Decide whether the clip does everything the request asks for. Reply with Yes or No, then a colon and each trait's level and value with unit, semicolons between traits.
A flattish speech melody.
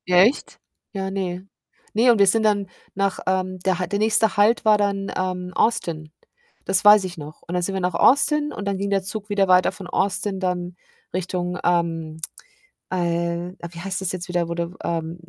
Yes: narrow, 2.3 semitones